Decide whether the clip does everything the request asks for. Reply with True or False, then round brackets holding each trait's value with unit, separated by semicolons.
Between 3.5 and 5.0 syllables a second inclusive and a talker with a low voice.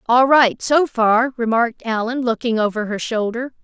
False (4.7 syllables/s; 235 Hz)